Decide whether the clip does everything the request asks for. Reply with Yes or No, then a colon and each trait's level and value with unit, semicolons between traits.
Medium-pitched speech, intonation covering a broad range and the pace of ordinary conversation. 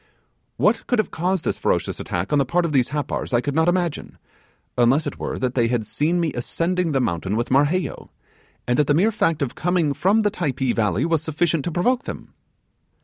No: medium, 150 Hz; wide, 5.7 semitones; fast, 210 wpm